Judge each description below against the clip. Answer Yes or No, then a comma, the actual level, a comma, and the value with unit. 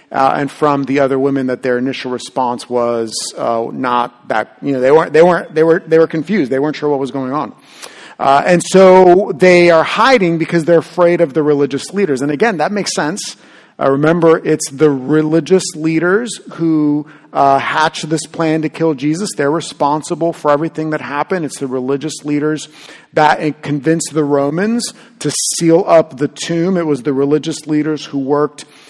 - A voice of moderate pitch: Yes, medium, 155 Hz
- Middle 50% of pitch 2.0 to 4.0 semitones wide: Yes, average, 2.9 semitones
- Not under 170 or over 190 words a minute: Yes, average, 185 wpm